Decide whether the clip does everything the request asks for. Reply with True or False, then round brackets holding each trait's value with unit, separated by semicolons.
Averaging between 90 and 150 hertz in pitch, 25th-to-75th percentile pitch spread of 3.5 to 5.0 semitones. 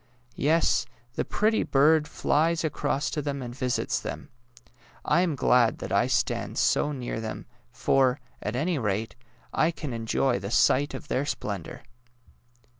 True (135 Hz; 4.3 semitones)